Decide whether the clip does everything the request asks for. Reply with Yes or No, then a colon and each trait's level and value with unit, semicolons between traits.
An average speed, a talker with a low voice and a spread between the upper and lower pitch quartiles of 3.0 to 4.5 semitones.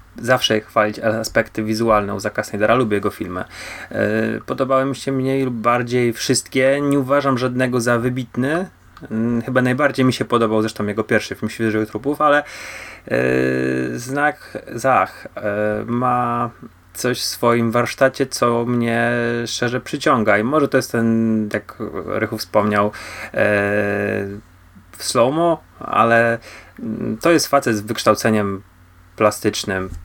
Yes: average, 130 wpm; low, 115 Hz; average, 3.3 semitones